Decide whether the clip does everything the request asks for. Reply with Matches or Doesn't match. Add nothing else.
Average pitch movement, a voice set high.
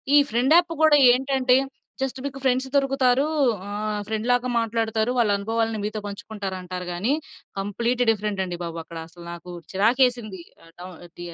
Matches